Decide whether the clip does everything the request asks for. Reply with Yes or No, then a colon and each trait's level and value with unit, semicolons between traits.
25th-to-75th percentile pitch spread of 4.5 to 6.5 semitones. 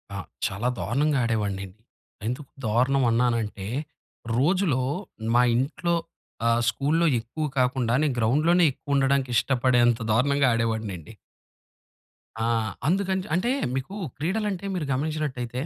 Yes: average, 4.8 semitones